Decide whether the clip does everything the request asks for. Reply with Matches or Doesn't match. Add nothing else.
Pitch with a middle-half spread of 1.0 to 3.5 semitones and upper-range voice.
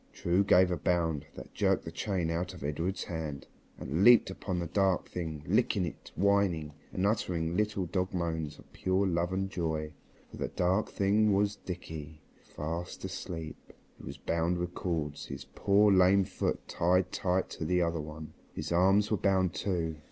Doesn't match